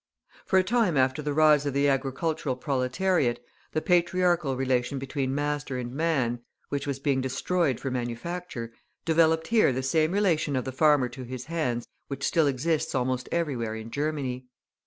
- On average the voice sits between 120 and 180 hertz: Yes, medium, 140 Hz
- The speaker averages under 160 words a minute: No, average, 165 wpm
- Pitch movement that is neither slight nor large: Yes, average, 4.0 semitones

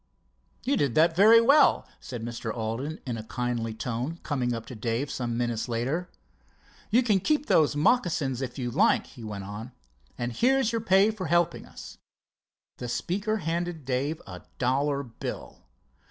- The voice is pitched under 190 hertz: Yes, low, 135 Hz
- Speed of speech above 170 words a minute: No, average, 165 wpm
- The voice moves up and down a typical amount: No, wide, 6.8 semitones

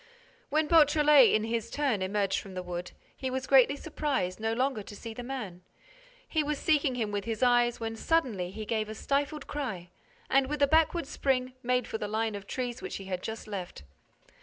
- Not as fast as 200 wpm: No, fast, 205 wpm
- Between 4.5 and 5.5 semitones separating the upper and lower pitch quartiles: Yes, average, 5.0 semitones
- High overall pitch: Yes, high, 240 Hz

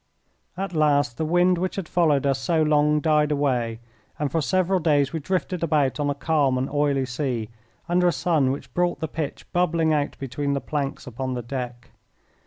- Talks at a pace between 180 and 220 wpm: Yes, average, 195 wpm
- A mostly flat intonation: No, average, 3.3 semitones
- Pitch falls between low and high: Yes, medium, 150 Hz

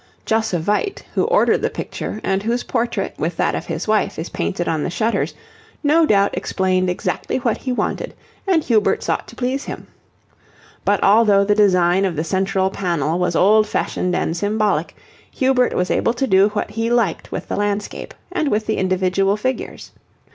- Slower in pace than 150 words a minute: No, average, 180 wpm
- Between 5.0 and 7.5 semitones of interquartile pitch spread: No, average, 3.9 semitones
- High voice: Yes, high, 205 Hz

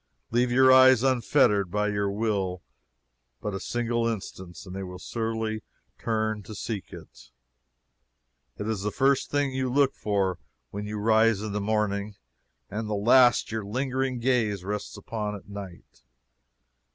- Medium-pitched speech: No, low, 110 Hz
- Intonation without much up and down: No, average, 3.1 semitones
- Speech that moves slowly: No, average, 150 wpm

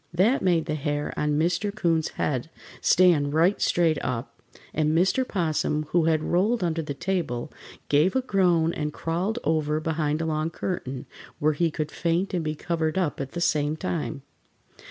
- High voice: No, medium, 160 Hz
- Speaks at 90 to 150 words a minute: No, average, 175 wpm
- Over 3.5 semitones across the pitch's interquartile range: No, average, 2.7 semitones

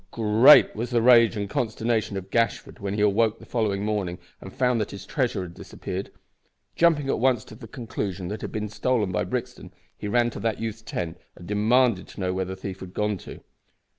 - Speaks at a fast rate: Yes, fast, 215 wpm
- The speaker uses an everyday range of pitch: Yes, average, 3.2 semitones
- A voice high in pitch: No, low, 105 Hz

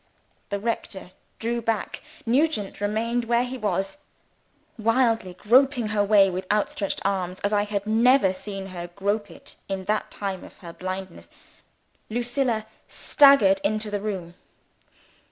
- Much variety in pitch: No, average, 3.2 semitones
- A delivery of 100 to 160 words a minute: Yes, slow, 135 wpm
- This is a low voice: No, high, 210 Hz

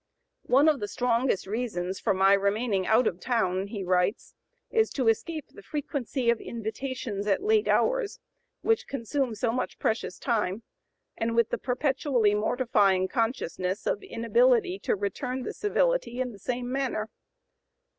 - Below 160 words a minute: Yes, average, 150 wpm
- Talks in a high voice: Yes, high, 235 Hz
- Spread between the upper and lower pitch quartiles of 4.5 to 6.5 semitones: Yes, average, 4.9 semitones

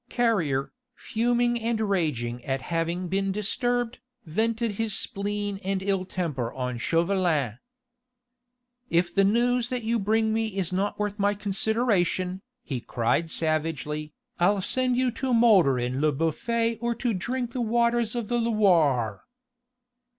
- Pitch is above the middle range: Yes, high, 200 Hz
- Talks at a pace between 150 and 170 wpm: No, average, 140 wpm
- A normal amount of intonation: No, wide, 6.0 semitones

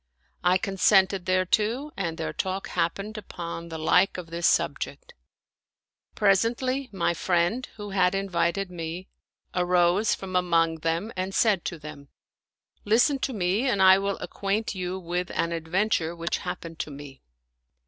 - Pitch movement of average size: Yes, average, 3.0 semitones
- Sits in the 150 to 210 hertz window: Yes, medium, 185 Hz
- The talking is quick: No, average, 150 wpm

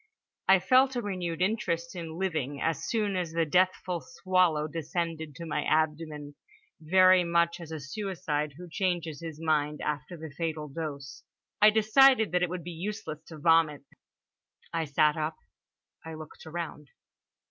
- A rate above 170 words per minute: No, average, 155 wpm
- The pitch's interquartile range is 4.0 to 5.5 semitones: No, average, 3.1 semitones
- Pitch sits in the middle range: Yes, medium, 165 Hz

